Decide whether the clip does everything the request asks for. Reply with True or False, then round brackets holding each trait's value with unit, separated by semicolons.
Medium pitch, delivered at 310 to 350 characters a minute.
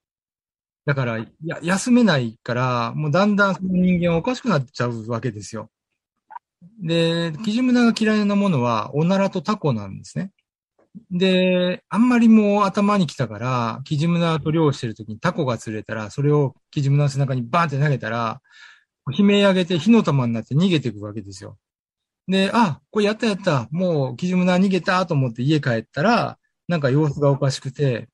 False (160 Hz; 360 characters per minute)